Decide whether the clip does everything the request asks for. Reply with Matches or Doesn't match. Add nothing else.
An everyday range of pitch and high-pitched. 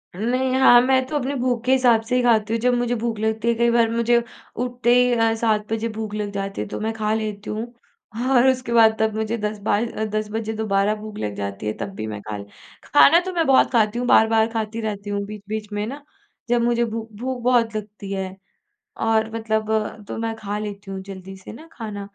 Doesn't match